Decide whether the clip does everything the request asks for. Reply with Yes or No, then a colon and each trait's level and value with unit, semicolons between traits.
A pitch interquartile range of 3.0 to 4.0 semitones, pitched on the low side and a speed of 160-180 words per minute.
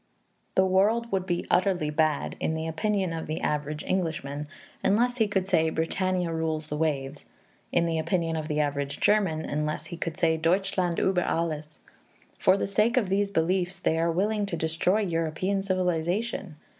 No: average, 3.4 semitones; medium, 170 Hz; average, 170 wpm